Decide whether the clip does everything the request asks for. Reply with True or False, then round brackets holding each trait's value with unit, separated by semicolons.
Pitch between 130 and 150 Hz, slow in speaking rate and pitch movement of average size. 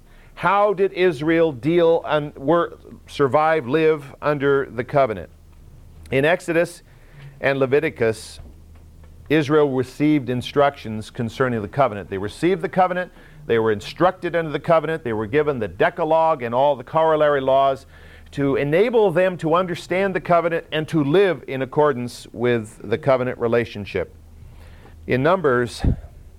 False (140 Hz; 130 wpm; 6.5 semitones)